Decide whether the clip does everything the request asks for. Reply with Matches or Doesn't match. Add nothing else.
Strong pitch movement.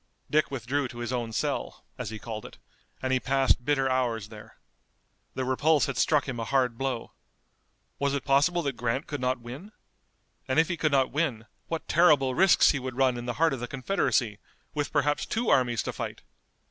Doesn't match